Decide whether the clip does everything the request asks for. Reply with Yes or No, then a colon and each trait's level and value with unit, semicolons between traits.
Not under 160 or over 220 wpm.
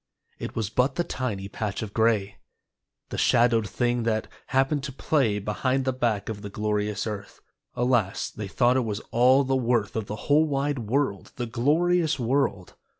Yes: average, 175 wpm